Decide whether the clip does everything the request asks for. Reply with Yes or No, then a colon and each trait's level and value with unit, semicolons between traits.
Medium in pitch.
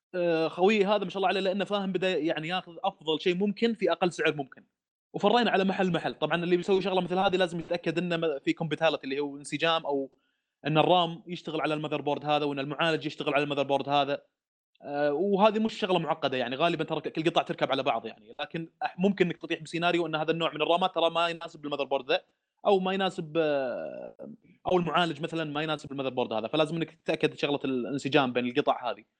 Yes: medium, 165 Hz